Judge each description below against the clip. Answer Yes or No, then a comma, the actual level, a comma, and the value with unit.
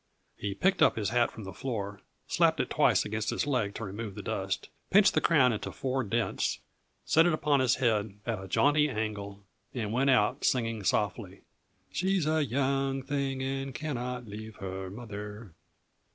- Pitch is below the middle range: Yes, low, 120 Hz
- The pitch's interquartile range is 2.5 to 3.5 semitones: No, average, 4.7 semitones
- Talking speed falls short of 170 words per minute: No, average, 175 wpm